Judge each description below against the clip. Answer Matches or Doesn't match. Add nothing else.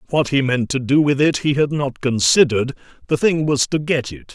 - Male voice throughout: Matches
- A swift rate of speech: Matches